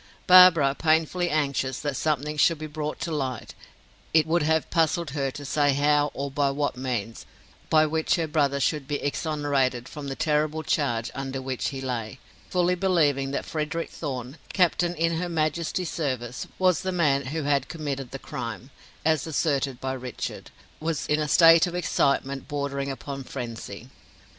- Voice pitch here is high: No, medium, 145 Hz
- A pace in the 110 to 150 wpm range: No, average, 165 wpm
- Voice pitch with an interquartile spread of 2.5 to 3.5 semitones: Yes, average, 2.9 semitones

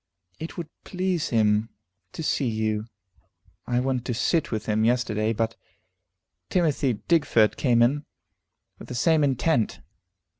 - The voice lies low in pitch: Yes, low, 125 Hz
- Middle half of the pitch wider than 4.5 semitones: Yes, wide, 5.6 semitones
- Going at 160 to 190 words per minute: No, slow, 135 wpm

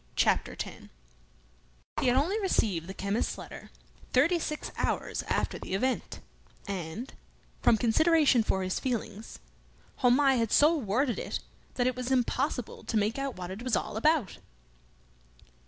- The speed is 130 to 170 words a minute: Yes, average, 145 wpm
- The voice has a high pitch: Yes, high, 245 Hz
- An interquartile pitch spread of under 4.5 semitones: No, average, 4.8 semitones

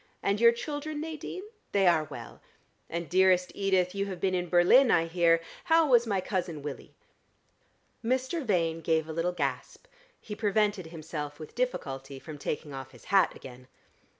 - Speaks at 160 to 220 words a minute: Yes, average, 165 wpm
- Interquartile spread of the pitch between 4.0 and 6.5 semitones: Yes, average, 5.1 semitones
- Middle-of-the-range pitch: Yes, medium, 180 Hz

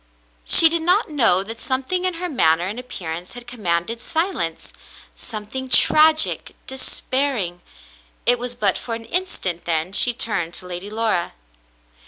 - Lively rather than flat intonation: Yes, wide, 7.4 semitones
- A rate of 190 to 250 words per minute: No, average, 160 wpm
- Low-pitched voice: No, high, 230 Hz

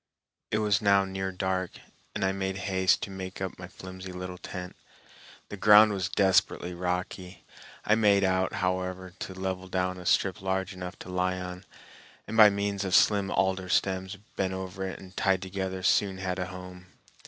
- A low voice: Yes, very low, 95 Hz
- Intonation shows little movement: Yes, narrow, 0.9 semitones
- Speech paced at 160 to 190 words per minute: Yes, average, 180 wpm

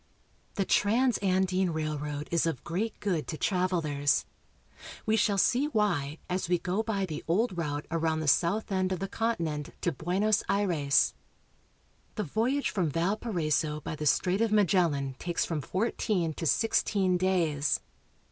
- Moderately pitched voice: Yes, medium, 180 Hz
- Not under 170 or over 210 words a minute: No, average, 150 wpm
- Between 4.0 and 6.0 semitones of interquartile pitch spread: Yes, average, 4.7 semitones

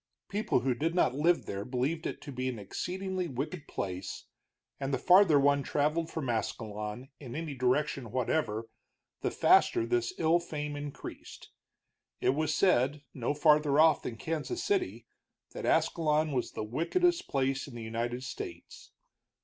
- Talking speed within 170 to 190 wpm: No, average, 155 wpm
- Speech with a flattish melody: No, average, 4.7 semitones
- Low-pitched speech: No, medium, 145 Hz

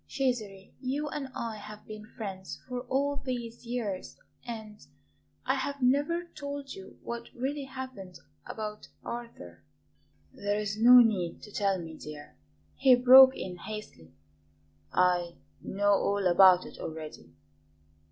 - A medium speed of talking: No, slow, 130 wpm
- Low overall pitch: No, high, 215 Hz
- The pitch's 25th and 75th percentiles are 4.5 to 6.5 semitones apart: Yes, average, 5.1 semitones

